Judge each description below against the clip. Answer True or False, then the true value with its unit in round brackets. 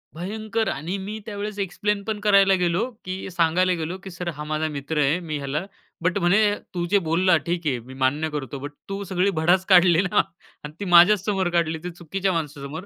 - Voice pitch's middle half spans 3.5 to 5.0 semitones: True (3.8 semitones)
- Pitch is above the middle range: False (175 Hz)